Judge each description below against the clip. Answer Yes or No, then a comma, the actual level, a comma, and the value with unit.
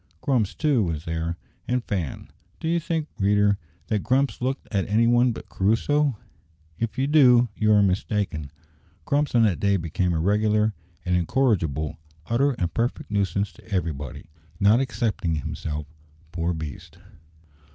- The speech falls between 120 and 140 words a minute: No, average, 150 wpm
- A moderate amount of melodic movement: No, wide, 6.1 semitones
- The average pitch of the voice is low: Yes, low, 105 Hz